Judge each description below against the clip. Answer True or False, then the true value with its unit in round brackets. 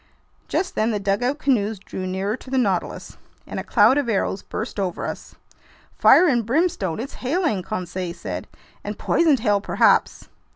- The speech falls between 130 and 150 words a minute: False (165 wpm)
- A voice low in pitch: False (215 Hz)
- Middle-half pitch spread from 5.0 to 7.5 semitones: True (5.5 semitones)